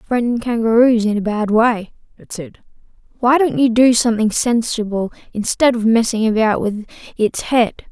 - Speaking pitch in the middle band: No, high, 225 Hz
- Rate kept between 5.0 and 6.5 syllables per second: No, 4.6 syllables/s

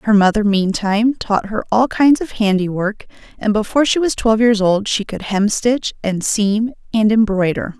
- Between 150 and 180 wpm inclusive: Yes, average, 175 wpm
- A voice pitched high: Yes, high, 215 Hz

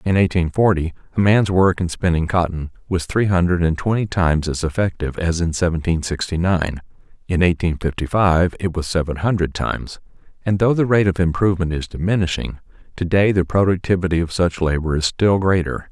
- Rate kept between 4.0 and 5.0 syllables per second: No, 5.6 syllables/s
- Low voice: Yes, very low, 90 Hz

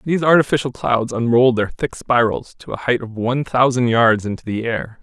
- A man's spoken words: Yes, male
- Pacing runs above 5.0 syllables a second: Yes, 5.5 syllables/s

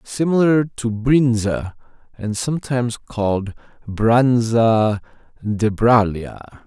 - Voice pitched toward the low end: Yes, low, 115 Hz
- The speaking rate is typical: No, slow, 80 wpm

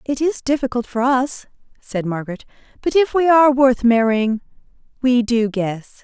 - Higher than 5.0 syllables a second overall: No, 4.9 syllables/s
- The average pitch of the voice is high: Yes, very high, 250 Hz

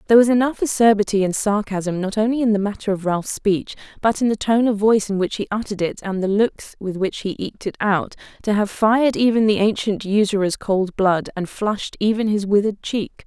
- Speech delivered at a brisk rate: Yes, fast, 220 wpm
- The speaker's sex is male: No, female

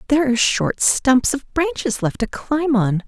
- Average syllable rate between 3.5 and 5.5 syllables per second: Yes, 4.6 syllables/s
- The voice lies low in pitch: No, very high, 250 Hz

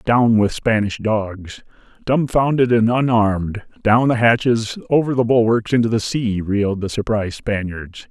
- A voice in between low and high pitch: No, low, 115 Hz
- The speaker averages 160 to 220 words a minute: No, average, 150 wpm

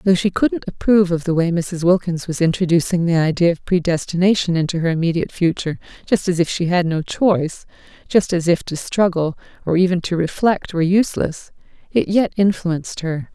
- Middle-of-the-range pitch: Yes, medium, 175 Hz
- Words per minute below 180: No, average, 185 wpm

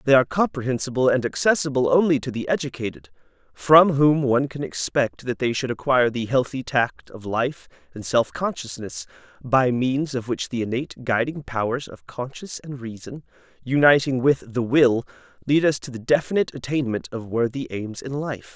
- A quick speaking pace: No, average, 170 wpm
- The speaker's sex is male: Yes, male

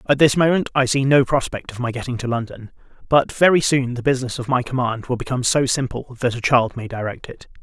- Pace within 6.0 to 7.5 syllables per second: Yes, 6.1 syllables/s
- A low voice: Yes, low, 130 Hz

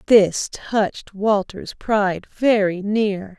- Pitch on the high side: Yes, high, 205 Hz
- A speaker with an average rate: No, slow, 105 wpm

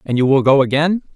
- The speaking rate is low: No, fast, 260 wpm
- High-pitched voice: No, medium, 145 Hz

